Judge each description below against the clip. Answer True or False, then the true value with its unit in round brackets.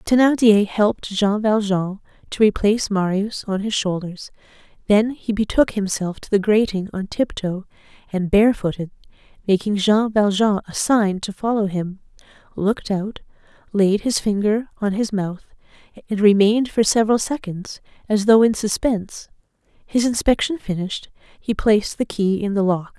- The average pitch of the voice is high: True (205 Hz)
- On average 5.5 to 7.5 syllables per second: False (4.8 syllables/s)